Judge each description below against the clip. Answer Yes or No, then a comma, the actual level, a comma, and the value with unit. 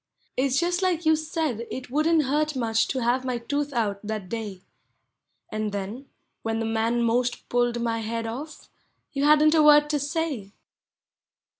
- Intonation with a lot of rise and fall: No, average, 4.9 semitones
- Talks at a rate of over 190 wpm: No, average, 170 wpm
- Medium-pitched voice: No, very high, 250 Hz